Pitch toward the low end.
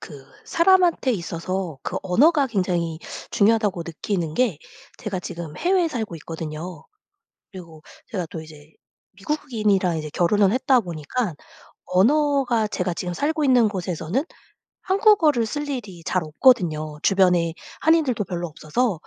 No: high, 190 Hz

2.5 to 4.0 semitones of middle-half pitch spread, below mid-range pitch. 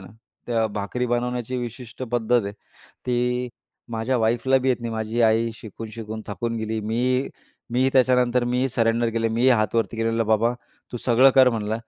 No: narrow, 1.8 semitones; low, 115 Hz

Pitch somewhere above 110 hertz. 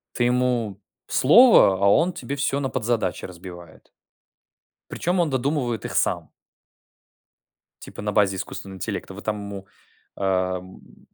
No: low, 105 Hz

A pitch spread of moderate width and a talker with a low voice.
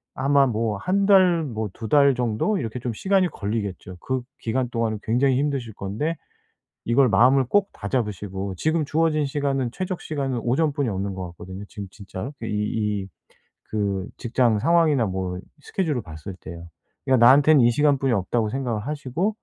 No: wide, 5.8 semitones; low, 125 Hz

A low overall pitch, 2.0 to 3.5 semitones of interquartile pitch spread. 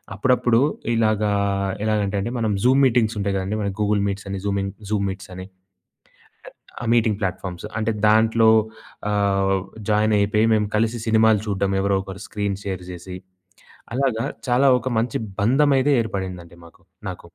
Yes: low, 105 Hz; narrow, 2.4 semitones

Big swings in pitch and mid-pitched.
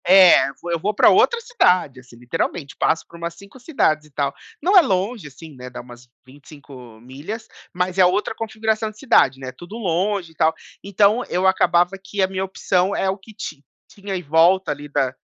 Yes: wide, 5.7 semitones; medium, 180 Hz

